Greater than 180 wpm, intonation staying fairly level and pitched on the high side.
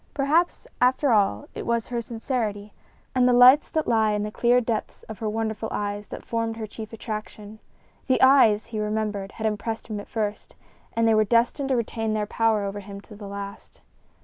Yes: average, 200 wpm; narrow, 2.1 semitones; high, 220 Hz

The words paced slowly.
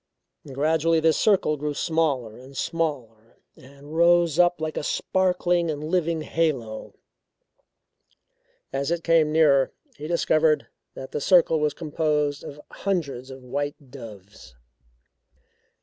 Yes: slow, 120 wpm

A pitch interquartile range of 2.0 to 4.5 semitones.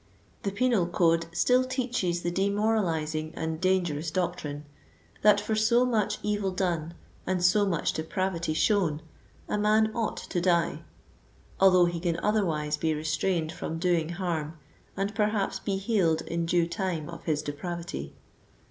Yes: average, 3.9 semitones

